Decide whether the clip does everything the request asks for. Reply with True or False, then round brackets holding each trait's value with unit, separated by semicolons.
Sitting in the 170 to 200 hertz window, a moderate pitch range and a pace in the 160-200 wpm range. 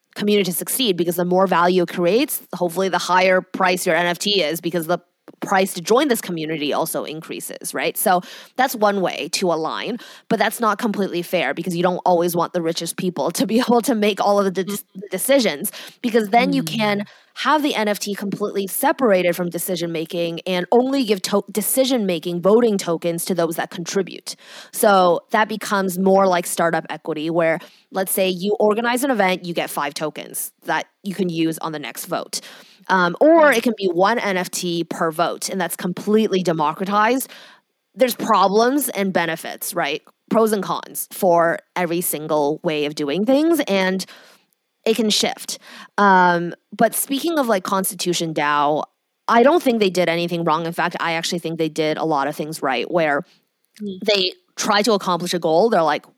True (190 Hz; 3.8 semitones; 185 wpm)